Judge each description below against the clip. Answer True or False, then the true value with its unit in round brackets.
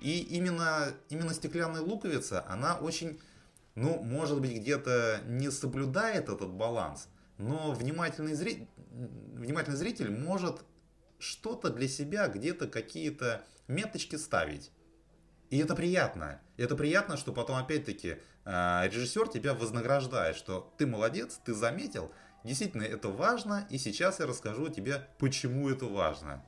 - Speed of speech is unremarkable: True (125 wpm)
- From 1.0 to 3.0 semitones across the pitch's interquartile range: False (5.6 semitones)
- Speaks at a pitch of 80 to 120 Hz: False (140 Hz)